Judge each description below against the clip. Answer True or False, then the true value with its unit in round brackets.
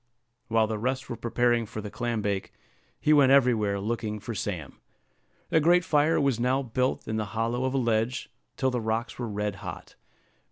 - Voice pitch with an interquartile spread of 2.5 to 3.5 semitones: True (3.2 semitones)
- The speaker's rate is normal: True (190 wpm)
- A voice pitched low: True (115 Hz)